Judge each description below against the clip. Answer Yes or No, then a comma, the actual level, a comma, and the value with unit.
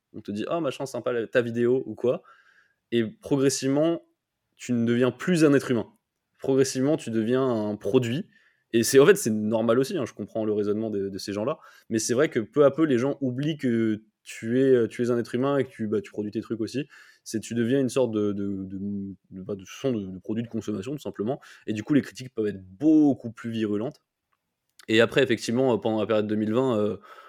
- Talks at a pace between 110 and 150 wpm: No, average, 200 wpm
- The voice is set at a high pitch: No, low, 115 Hz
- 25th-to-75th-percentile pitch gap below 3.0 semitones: No, average, 3.8 semitones